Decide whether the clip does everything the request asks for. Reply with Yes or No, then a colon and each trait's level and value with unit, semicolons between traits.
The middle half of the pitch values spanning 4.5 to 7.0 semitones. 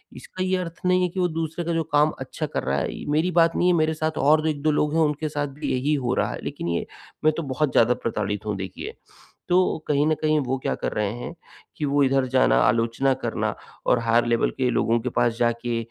Yes: average, 5.0 semitones